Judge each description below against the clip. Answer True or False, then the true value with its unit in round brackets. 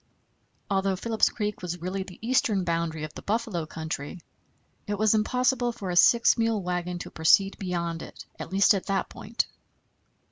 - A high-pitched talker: True (195 Hz)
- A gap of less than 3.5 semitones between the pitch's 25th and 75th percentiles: False (3.8 semitones)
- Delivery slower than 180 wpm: True (170 wpm)